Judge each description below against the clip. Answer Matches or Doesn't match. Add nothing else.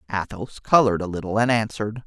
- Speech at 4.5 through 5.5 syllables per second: Doesn't match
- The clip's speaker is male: Matches